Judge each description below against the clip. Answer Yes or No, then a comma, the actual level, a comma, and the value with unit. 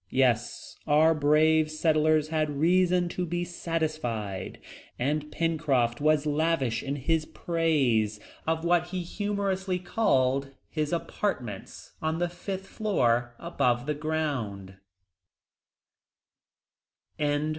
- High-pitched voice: No, medium, 155 Hz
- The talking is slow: Yes, slow, 100 wpm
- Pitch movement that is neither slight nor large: Yes, average, 4.3 semitones